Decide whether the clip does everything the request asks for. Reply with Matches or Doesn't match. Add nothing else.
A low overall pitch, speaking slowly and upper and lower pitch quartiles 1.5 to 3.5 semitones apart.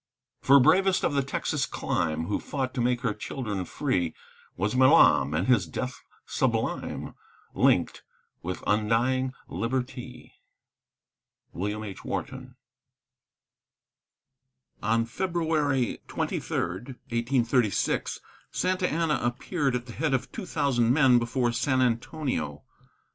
Doesn't match